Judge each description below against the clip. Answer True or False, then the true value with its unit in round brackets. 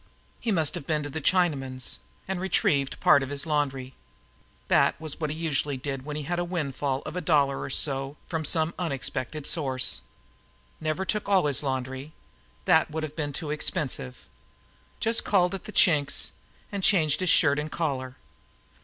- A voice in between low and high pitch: True (150 Hz)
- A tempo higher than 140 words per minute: True (180 wpm)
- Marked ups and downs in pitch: False (3.5 semitones)